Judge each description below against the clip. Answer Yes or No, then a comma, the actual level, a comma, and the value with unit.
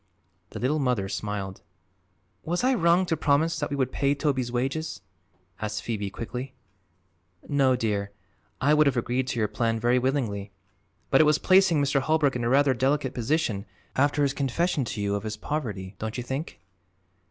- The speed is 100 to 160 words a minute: No, average, 175 wpm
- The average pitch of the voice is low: Yes, low, 130 Hz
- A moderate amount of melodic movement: Yes, average, 4.7 semitones